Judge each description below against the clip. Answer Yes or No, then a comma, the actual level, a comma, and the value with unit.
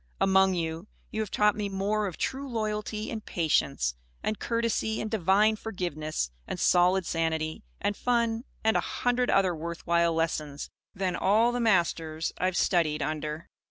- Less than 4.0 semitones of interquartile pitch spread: No, average, 4.8 semitones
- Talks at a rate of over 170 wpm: No, average, 160 wpm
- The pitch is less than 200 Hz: Yes, high, 190 Hz